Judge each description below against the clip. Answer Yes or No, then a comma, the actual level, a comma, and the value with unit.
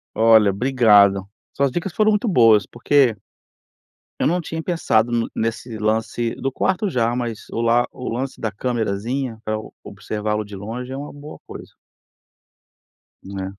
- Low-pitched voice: Yes, low, 115 Hz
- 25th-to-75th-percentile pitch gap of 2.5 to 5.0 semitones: Yes, average, 3.8 semitones